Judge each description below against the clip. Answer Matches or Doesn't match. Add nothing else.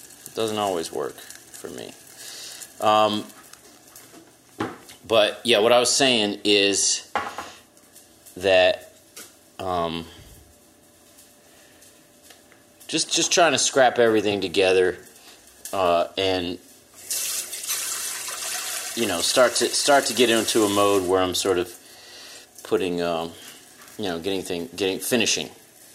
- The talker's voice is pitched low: Matches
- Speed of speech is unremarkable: Doesn't match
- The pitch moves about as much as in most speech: Matches